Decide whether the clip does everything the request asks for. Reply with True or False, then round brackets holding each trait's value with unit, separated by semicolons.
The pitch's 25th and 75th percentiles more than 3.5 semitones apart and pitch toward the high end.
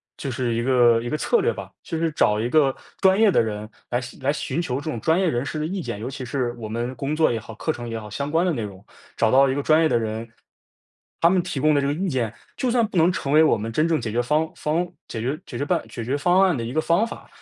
False (5.4 semitones; 140 Hz)